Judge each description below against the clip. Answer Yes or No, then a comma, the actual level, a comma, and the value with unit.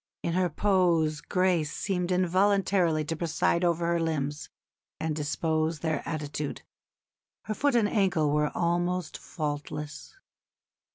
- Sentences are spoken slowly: Yes, slow, 120 wpm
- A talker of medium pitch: Yes, medium, 170 Hz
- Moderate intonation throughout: Yes, average, 3.0 semitones